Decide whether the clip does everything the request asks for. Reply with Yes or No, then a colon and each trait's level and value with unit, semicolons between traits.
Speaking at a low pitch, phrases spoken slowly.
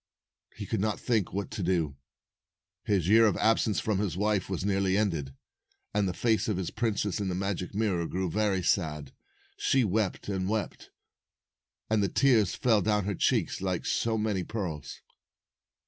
No: low, 100 Hz; average, 170 wpm